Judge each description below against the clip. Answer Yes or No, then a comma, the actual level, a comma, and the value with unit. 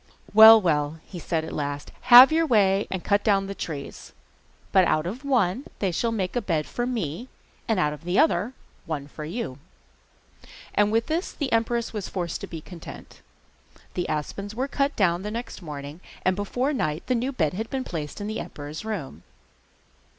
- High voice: Yes, high, 195 Hz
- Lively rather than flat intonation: Yes, wide, 6.4 semitones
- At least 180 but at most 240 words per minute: Yes, average, 185 wpm